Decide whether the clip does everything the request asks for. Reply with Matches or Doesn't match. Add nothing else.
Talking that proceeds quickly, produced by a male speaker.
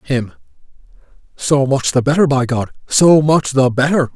Doesn't match